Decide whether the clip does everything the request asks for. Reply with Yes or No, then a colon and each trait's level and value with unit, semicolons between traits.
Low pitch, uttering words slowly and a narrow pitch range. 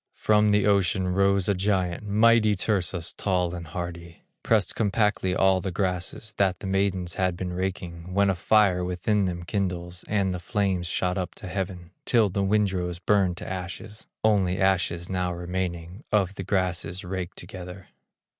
No: very low, 95 Hz; average, 165 wpm; narrow, 2.1 semitones